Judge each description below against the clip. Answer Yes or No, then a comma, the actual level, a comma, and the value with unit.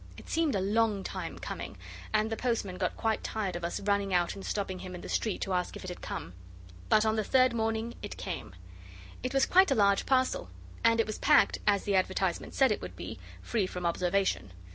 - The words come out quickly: Yes, fast, 225 wpm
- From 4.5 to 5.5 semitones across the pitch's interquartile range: No, average, 3.5 semitones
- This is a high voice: Yes, high, 205 Hz